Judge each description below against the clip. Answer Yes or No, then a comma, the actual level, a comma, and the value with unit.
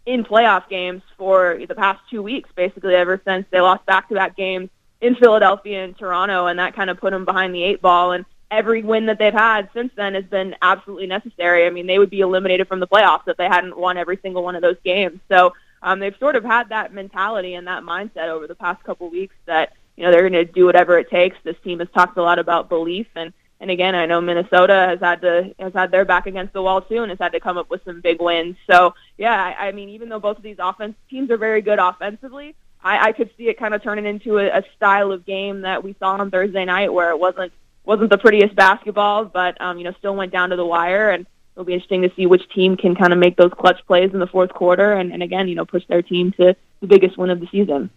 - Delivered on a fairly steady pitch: Yes, narrow, 2.0 semitones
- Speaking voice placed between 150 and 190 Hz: Yes, medium, 185 Hz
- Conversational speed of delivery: No, fast, 265 wpm